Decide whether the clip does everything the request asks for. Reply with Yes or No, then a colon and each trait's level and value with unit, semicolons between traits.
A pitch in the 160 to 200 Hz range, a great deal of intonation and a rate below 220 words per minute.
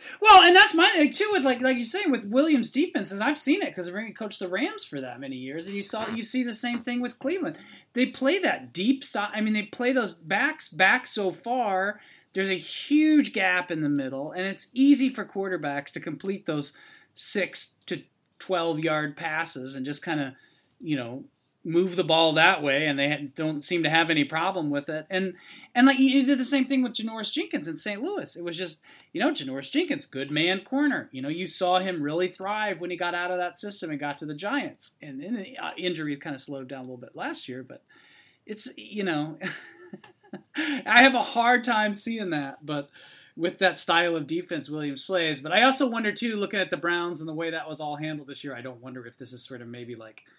No: medium, 185 Hz; wide, 8.6 semitones; fast, 230 wpm